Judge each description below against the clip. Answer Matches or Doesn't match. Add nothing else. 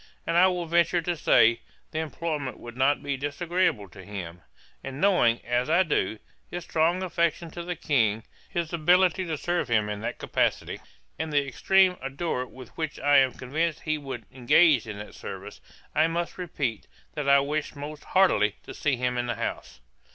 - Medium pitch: Matches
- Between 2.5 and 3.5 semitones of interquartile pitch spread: Doesn't match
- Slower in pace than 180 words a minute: Doesn't match